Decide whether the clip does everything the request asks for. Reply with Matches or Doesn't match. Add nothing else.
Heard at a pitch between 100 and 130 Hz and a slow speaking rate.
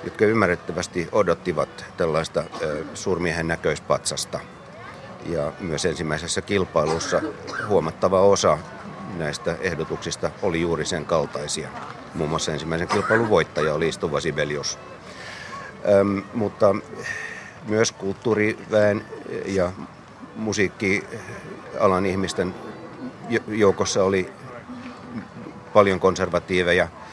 Doesn't match